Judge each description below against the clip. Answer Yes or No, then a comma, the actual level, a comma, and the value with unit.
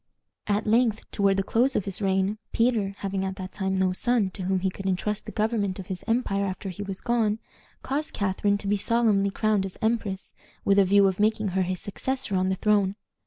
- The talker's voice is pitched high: Yes, high, 200 Hz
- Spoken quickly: Yes, fast, 215 wpm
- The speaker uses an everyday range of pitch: No, narrow, 2.2 semitones